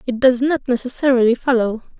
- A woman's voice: Yes, female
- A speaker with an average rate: Yes, average, 150 wpm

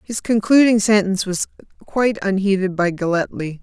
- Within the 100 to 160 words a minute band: Yes, slow, 135 wpm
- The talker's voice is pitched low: No, high, 200 Hz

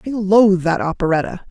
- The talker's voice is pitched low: No, high, 190 Hz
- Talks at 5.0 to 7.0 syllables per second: Yes, 6.0 syllables/s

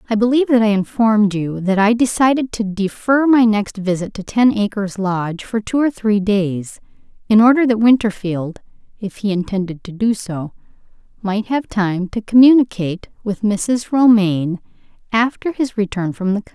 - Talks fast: No, average, 170 wpm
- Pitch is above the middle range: Yes, high, 210 Hz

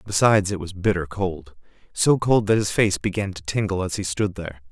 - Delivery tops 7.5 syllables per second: No, 5.6 syllables/s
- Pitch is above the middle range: No, very low, 95 Hz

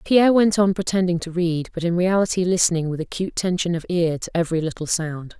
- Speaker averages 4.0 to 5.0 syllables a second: No, 6.2 syllables/s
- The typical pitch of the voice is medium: Yes, medium, 175 Hz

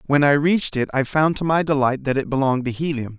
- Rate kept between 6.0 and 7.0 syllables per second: Yes, 6.3 syllables/s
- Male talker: Yes, male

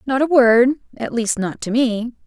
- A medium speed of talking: Yes, average, 185 wpm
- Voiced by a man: No, female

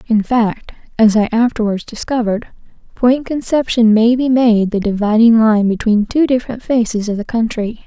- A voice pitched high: Yes, high, 230 Hz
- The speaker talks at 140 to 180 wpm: Yes, average, 160 wpm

